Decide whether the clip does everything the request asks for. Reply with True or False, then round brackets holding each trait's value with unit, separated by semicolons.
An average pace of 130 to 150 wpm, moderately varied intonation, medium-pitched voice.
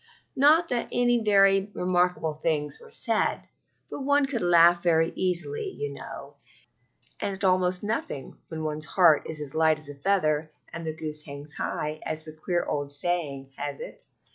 False (165 wpm; 4.4 semitones; 170 Hz)